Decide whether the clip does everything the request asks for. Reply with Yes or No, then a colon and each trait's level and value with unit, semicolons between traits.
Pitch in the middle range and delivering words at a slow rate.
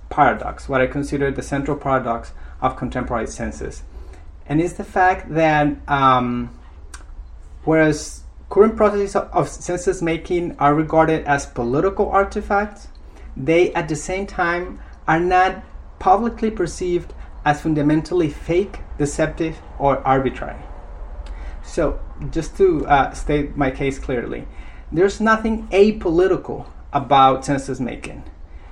Yes: medium, 150 Hz; slow, 120 wpm